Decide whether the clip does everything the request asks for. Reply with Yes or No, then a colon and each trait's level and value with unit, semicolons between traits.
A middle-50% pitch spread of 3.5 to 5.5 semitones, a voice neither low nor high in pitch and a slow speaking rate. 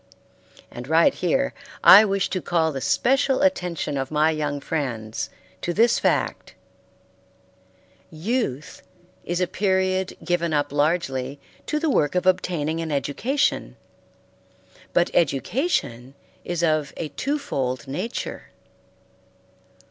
Yes: average, 4.7 semitones; medium, 165 Hz; slow, 120 wpm